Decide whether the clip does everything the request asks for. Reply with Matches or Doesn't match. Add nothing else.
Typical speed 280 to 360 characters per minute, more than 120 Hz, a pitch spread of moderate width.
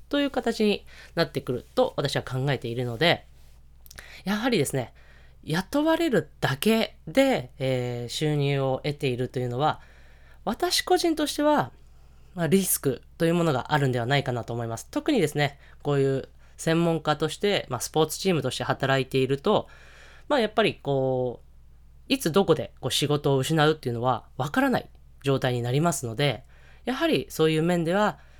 Doesn't match